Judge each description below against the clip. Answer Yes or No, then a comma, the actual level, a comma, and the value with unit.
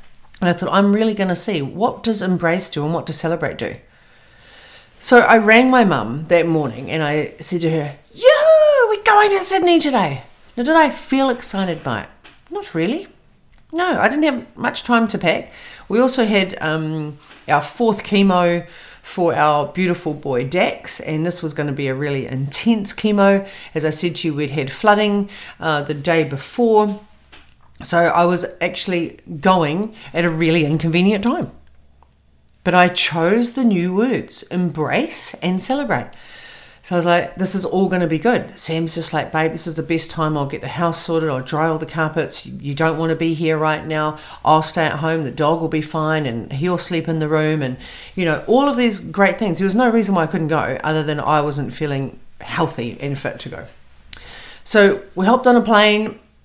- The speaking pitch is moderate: Yes, medium, 170 Hz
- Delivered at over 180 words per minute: Yes, average, 200 wpm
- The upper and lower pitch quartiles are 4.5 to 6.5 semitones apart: Yes, average, 5.2 semitones